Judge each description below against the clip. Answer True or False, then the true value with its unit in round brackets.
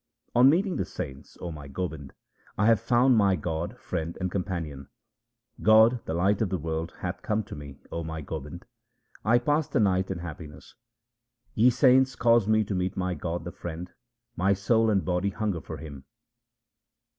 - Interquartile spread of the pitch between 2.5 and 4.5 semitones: False (5.0 semitones)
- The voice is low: True (95 Hz)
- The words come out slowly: False (180 wpm)